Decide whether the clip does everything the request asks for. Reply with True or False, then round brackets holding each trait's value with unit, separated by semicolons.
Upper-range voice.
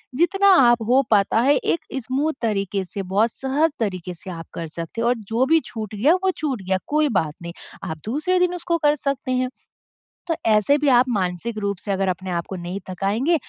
True (230 Hz)